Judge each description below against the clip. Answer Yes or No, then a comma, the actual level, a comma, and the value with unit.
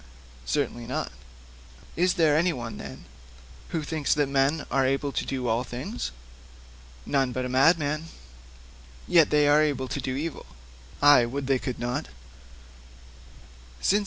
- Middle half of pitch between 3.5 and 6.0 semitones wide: No, average, 3.0 semitones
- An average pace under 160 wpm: Yes, slow, 135 wpm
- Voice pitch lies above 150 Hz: No, medium, 140 Hz